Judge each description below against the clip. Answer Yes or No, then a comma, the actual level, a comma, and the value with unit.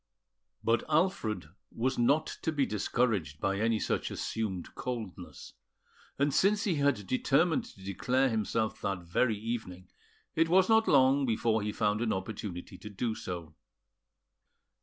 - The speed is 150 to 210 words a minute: No, average, 140 wpm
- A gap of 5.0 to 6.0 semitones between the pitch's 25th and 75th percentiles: Yes, wide, 5.6 semitones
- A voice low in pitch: Yes, low, 115 Hz